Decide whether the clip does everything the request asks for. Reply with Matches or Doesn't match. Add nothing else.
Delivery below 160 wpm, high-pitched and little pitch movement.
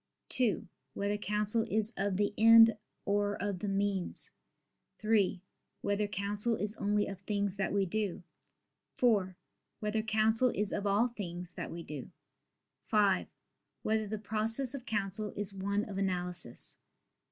Matches